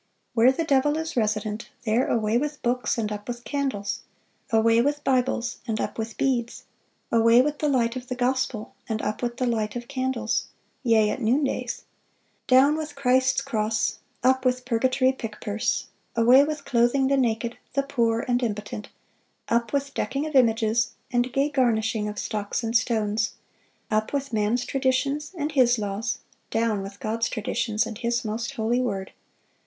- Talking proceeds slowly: No, average, 170 wpm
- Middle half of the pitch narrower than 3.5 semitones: Yes, average, 3.0 semitones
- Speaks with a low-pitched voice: No, high, 240 Hz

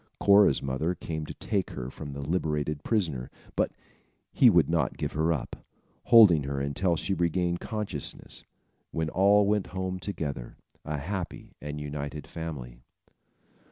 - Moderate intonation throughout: Yes, average, 4.5 semitones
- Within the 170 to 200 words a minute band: No, average, 145 wpm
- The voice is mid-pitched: No, very low, 80 Hz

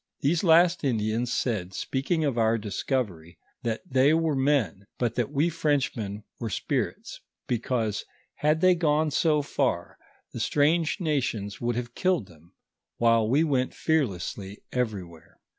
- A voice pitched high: No, low, 125 Hz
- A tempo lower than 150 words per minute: Yes, average, 140 wpm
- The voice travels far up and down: Yes, wide, 5.9 semitones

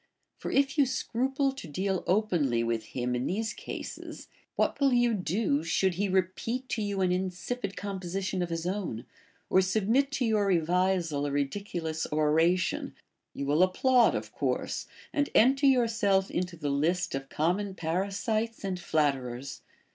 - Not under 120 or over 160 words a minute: Yes, average, 155 wpm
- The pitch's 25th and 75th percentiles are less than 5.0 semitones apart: No, average, 5.3 semitones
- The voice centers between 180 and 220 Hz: Yes, medium, 185 Hz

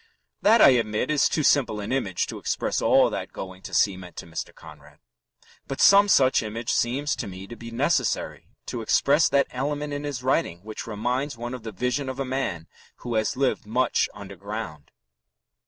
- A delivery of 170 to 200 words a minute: Yes, average, 190 wpm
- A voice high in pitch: No, low, 120 Hz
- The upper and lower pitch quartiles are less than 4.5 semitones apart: No, average, 5.1 semitones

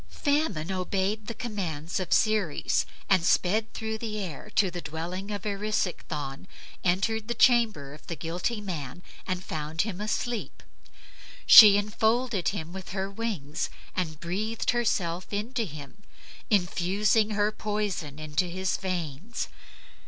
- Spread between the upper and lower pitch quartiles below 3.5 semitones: No, average, 4.2 semitones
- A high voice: Yes, high, 195 Hz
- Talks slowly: Yes, slow, 130 wpm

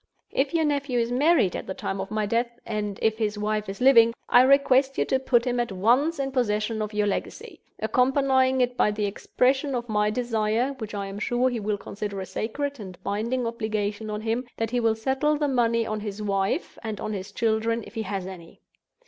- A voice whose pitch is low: No, high, 230 Hz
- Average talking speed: No, fast, 215 wpm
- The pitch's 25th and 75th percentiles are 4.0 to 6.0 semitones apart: No, average, 3.5 semitones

